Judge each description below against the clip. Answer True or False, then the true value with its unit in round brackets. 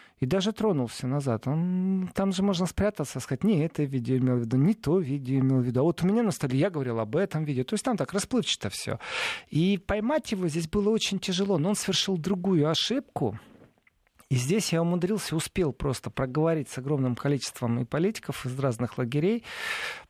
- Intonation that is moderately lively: False (6.8 semitones)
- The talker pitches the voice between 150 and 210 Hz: True (165 Hz)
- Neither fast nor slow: False (195 wpm)